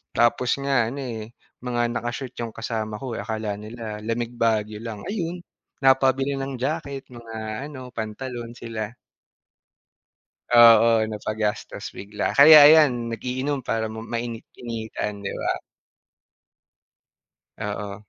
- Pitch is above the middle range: No, low, 115 Hz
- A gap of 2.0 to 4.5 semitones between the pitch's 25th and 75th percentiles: Yes, average, 3.1 semitones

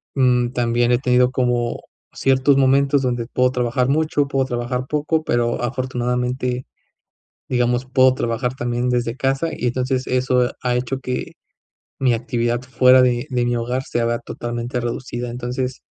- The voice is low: Yes, low, 125 Hz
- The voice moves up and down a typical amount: No, narrow, 1.3 semitones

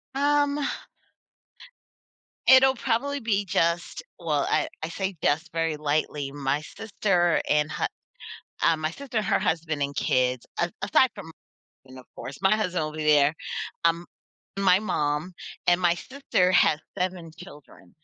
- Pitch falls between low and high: Yes, medium, 170 Hz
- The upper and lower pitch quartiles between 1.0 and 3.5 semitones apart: No, average, 5.1 semitones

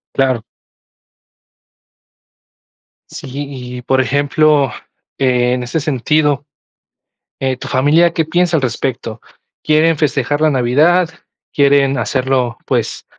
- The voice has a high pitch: No, medium, 140 Hz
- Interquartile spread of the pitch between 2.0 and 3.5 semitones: Yes, average, 3.2 semitones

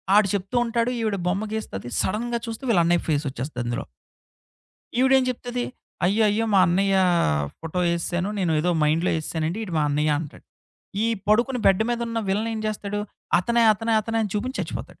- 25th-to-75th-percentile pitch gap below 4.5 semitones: No, average, 5.2 semitones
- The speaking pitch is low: No, high, 200 Hz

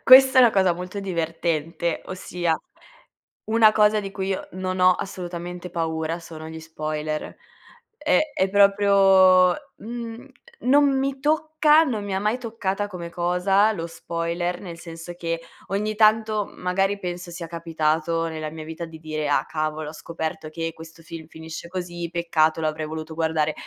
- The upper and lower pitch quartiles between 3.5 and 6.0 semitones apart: Yes, average, 3.8 semitones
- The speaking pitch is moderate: Yes, medium, 175 Hz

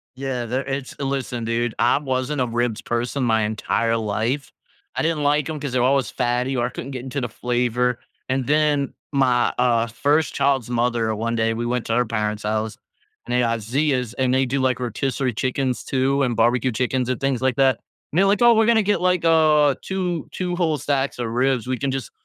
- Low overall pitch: Yes, low, 130 Hz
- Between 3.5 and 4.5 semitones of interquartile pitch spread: No, average, 2.8 semitones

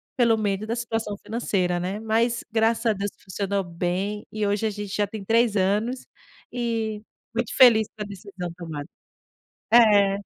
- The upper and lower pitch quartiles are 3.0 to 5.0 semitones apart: No, narrow, 2.5 semitones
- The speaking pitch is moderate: No, high, 210 Hz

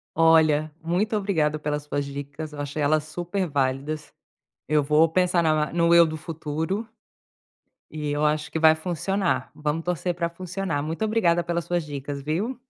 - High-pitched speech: No, medium, 160 Hz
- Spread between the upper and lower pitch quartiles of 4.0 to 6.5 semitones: No, narrow, 2.6 semitones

